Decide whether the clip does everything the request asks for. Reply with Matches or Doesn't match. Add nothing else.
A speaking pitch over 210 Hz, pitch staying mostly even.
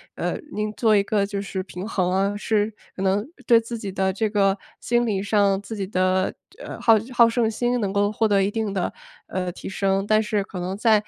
Doesn't match